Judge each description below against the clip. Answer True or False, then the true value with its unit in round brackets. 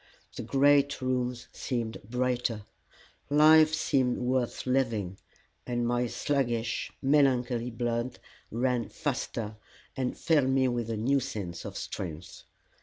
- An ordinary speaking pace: False (110 wpm)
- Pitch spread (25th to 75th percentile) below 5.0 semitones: True (2.5 semitones)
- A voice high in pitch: False (125 Hz)